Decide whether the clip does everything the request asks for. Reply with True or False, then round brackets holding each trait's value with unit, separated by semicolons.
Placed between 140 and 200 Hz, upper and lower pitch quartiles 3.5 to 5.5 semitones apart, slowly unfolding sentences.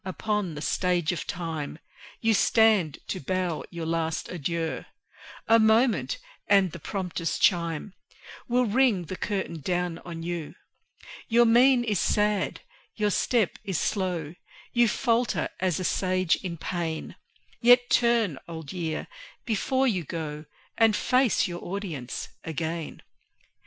True (185 Hz; 5.0 semitones; 130 wpm)